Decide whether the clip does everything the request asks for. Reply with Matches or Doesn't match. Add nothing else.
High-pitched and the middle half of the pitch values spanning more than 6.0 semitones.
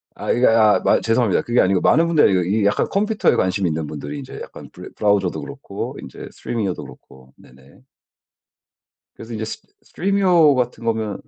Doesn't match